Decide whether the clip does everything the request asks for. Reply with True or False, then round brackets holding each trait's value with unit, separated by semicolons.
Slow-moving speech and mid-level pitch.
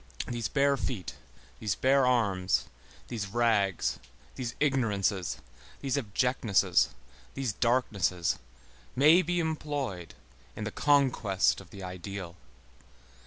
False (105 wpm; 115 Hz)